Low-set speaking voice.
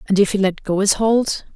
No: high, 200 Hz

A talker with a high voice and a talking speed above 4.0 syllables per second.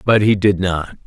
No: very low, 95 Hz; 4.4 syllables/s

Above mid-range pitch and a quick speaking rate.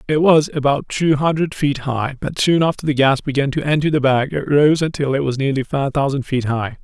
No: medium, 140 Hz; fast, 235 wpm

